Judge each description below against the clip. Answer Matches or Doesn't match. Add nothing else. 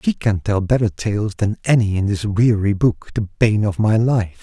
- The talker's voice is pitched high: Doesn't match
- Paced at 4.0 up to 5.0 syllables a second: Matches